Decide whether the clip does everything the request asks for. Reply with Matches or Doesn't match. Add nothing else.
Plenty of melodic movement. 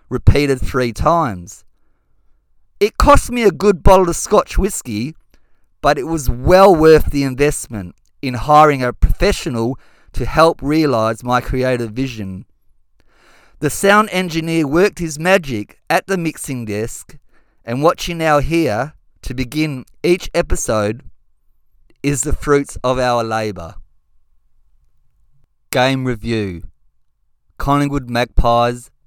Matches